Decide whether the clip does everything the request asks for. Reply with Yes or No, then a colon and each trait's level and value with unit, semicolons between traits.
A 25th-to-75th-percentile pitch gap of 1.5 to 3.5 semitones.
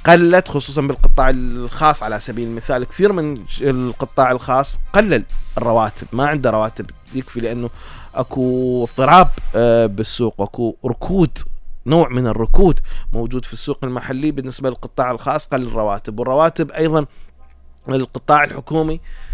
No: average, 4.0 semitones